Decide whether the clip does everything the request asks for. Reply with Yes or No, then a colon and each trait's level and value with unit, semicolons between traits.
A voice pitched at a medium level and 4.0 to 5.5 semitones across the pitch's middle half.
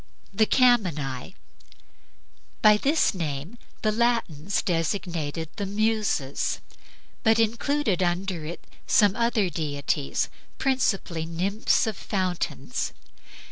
No: high, 195 Hz; average, 5.2 semitones